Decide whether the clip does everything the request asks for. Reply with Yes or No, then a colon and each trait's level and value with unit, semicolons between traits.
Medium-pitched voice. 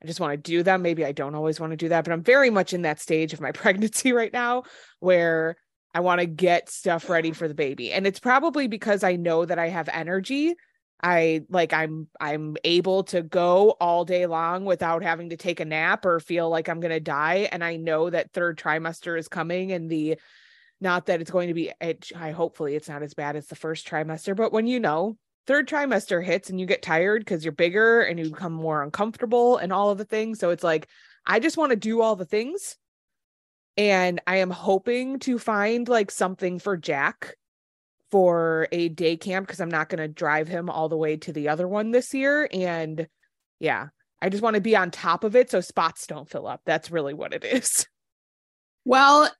Yes: medium, 175 Hz